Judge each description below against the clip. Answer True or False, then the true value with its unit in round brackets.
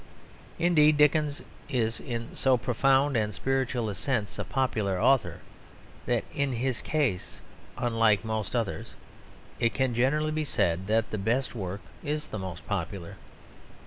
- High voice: False (120 Hz)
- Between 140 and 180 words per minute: True (145 wpm)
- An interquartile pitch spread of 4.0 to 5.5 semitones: True (4.4 semitones)